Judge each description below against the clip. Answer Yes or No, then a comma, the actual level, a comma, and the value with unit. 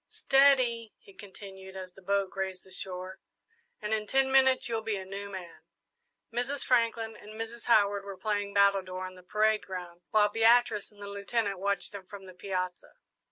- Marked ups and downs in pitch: No, average, 2.9 semitones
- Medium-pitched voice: No, high, 200 Hz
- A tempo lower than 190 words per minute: Yes, average, 180 wpm